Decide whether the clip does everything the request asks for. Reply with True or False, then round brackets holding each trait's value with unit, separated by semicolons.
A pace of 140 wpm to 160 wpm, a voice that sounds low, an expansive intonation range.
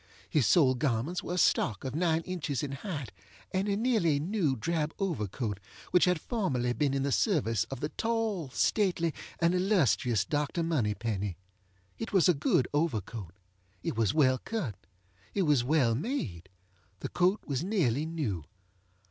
False (155 wpm; 150 Hz; 6.9 semitones)